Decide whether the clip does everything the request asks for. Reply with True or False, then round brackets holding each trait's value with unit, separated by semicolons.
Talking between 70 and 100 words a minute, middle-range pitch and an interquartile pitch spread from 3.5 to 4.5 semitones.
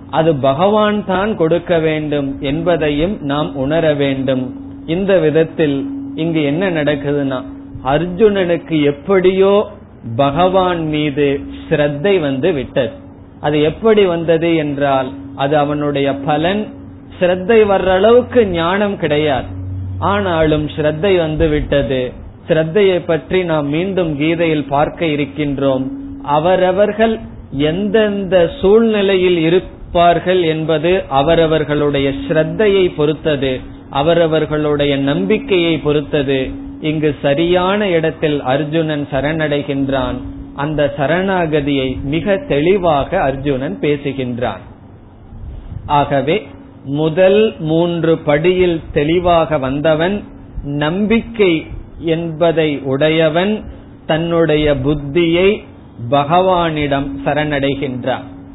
True (80 wpm; 155 Hz; 3.9 semitones)